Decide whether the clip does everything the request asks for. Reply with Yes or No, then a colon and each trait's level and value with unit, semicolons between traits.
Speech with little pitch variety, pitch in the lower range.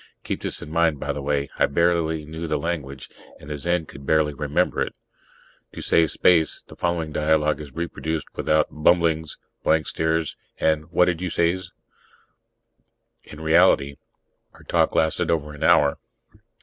Yes: narrow, 2.0 semitones; very low, 80 Hz